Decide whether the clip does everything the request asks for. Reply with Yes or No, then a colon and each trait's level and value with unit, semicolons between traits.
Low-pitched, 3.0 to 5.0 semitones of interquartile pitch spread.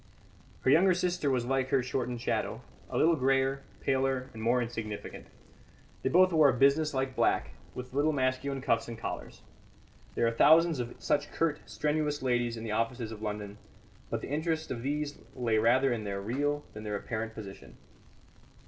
Yes: low, 130 Hz; average, 4.1 semitones